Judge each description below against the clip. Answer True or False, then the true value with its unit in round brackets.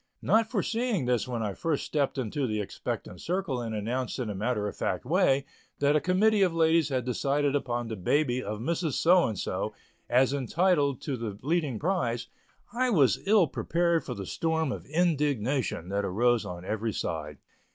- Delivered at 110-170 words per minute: False (185 wpm)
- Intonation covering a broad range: True (6.6 semitones)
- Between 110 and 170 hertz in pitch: True (135 Hz)